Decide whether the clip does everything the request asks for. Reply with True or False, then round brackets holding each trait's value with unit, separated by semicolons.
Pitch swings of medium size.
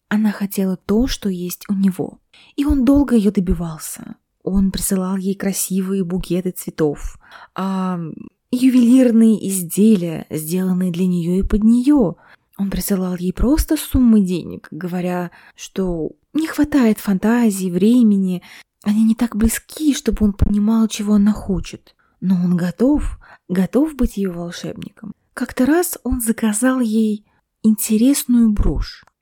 True (4.0 semitones)